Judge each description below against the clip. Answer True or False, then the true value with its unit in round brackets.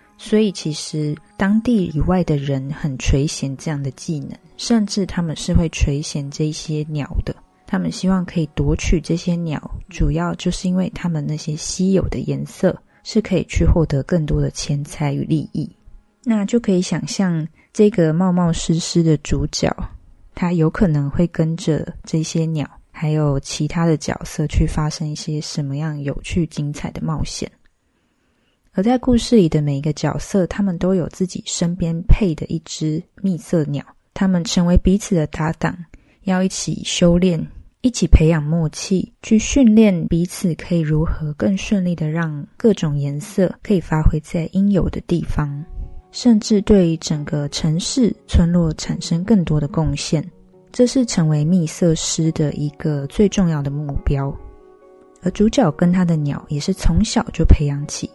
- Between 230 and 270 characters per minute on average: True (245 characters per minute)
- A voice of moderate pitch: True (170 Hz)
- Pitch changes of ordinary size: True (3.7 semitones)